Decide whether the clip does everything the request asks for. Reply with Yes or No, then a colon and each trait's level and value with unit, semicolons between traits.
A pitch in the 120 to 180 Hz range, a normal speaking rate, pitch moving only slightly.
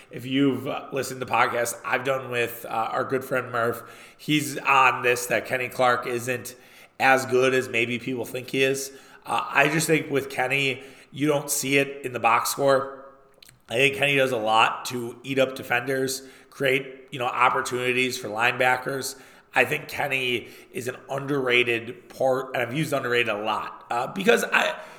Yes: low, 130 Hz; average, 180 wpm; narrow, 1.6 semitones